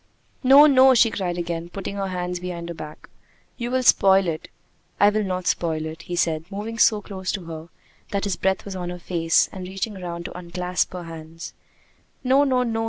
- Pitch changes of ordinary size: Yes, average, 3.4 semitones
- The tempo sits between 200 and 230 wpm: Yes, fast, 205 wpm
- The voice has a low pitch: No, medium, 185 Hz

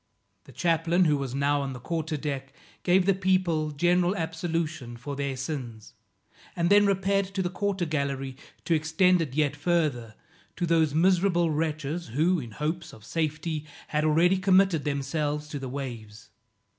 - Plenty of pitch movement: No, average, 3.8 semitones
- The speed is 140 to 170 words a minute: Yes, average, 160 wpm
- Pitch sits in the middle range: Yes, medium, 155 Hz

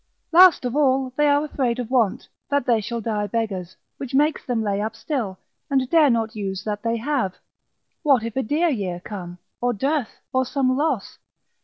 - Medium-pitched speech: No, high, 245 Hz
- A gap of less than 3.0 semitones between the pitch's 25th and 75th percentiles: No, average, 4.7 semitones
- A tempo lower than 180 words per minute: No, average, 190 wpm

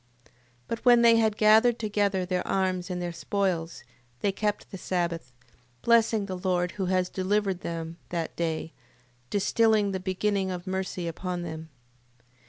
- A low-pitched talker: No, high, 190 Hz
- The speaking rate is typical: Yes, average, 155 wpm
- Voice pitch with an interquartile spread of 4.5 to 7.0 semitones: No, average, 2.8 semitones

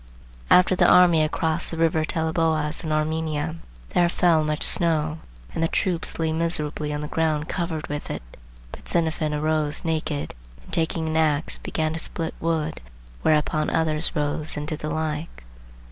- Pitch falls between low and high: Yes, medium, 160 Hz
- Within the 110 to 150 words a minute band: No, average, 165 wpm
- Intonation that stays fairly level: Yes, narrow, 1.3 semitones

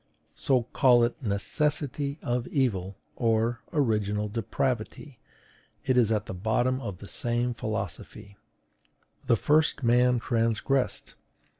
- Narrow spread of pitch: No, average, 3.0 semitones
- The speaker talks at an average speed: No, slow, 105 wpm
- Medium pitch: No, low, 120 Hz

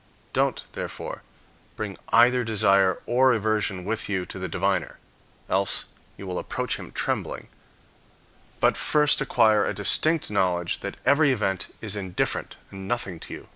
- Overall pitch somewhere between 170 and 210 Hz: No, low, 105 Hz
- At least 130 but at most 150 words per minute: Yes, average, 145 wpm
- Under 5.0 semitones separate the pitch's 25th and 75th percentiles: Yes, average, 3.7 semitones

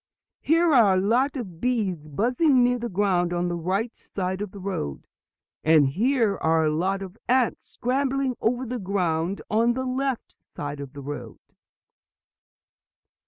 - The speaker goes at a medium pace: Yes, average, 160 wpm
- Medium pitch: No, high, 200 Hz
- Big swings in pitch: Yes, wide, 6.2 semitones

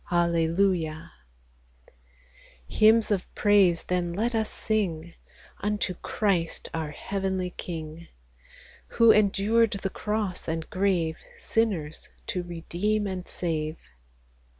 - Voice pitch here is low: No, medium, 185 Hz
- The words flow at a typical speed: No, slow, 100 wpm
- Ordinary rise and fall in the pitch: Yes, average, 3.8 semitones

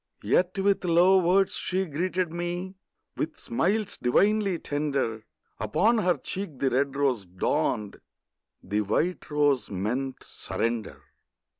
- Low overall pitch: No, medium, 155 Hz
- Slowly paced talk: Yes, slow, 120 wpm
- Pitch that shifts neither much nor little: No, wide, 6.9 semitones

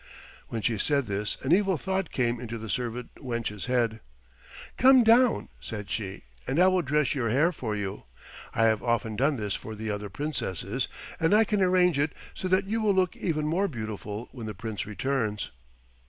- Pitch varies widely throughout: Yes, wide, 8.5 semitones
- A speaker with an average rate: Yes, average, 190 wpm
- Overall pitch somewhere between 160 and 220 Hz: No, low, 125 Hz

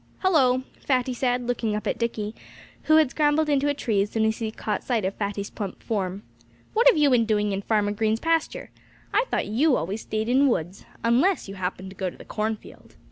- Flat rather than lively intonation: No, average, 4.8 semitones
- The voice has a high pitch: Yes, high, 225 Hz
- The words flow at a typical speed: No, fast, 220 wpm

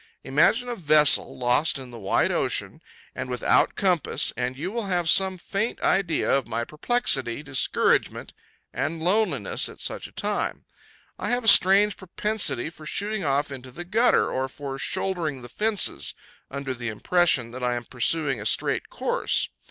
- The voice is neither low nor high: Yes, medium, 150 Hz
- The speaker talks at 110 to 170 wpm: Yes, average, 165 wpm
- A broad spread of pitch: Yes, wide, 6.9 semitones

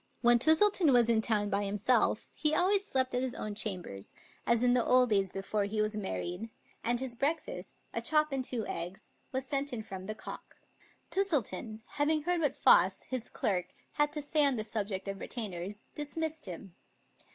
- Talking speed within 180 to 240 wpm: Yes, average, 190 wpm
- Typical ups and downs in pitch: No, wide, 5.9 semitones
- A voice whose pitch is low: No, high, 235 Hz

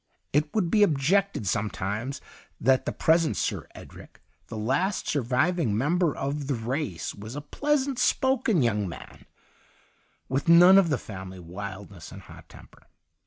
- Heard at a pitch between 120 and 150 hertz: Yes, medium, 140 Hz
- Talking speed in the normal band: Yes, average, 150 wpm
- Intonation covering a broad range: Yes, wide, 8.7 semitones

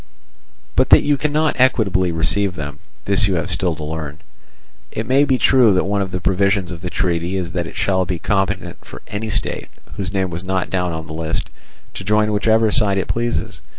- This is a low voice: Yes, very low, 95 Hz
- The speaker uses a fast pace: Yes, fast, 210 wpm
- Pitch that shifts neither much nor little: Yes, average, 3.5 semitones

